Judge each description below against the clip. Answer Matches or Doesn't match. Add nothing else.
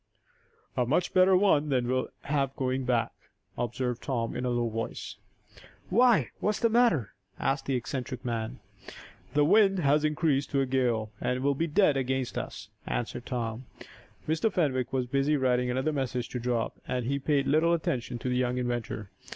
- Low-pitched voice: Matches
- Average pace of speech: Matches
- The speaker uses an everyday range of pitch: Matches